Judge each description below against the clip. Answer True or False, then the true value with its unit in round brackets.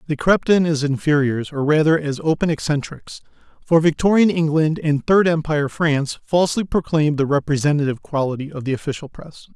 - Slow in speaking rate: False (170 wpm)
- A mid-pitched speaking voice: True (155 Hz)